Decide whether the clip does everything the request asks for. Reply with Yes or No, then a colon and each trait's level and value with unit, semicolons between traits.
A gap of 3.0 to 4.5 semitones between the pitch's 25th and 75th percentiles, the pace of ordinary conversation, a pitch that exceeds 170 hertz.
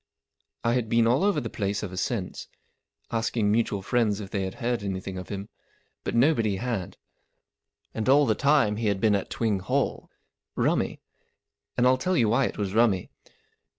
No: average, 3.5 semitones; average, 180 wpm; low, 110 Hz